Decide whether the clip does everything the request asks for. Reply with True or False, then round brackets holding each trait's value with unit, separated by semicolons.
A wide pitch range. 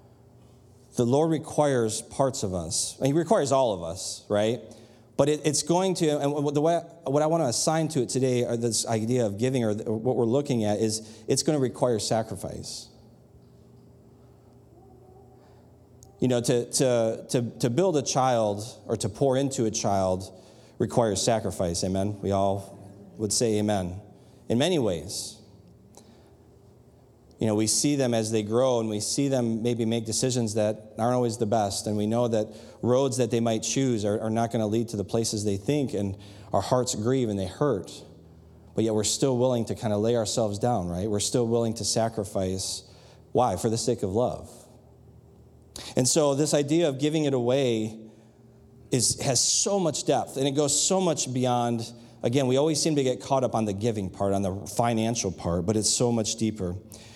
False (3.3 semitones)